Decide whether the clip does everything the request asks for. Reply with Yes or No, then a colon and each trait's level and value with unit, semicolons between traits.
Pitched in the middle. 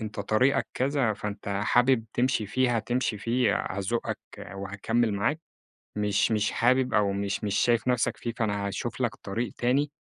No: low, 115 Hz